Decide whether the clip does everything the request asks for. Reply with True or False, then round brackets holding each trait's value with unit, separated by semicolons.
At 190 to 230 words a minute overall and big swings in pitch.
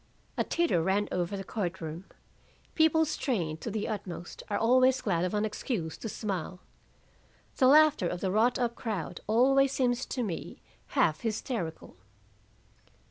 False (150 wpm; 5.9 semitones)